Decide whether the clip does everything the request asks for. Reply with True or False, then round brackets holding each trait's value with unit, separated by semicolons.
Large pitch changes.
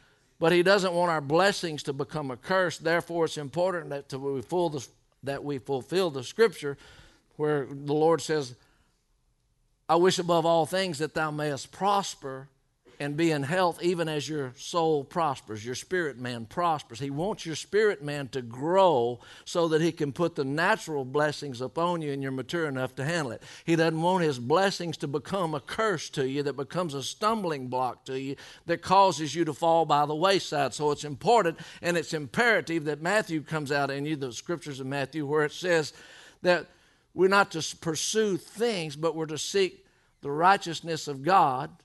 False (3.7 semitones)